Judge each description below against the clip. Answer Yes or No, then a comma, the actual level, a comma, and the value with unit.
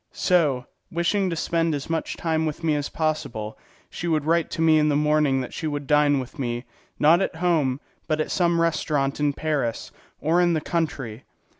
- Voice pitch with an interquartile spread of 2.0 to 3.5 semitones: Yes, average, 2.7 semitones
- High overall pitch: No, medium, 155 Hz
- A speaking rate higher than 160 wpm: Yes, average, 195 wpm